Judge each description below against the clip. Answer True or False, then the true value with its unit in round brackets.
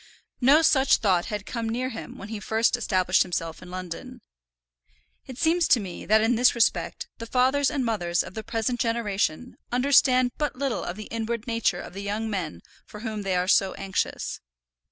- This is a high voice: True (225 Hz)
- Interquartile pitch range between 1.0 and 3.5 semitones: False (4.4 semitones)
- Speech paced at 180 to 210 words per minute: True (190 wpm)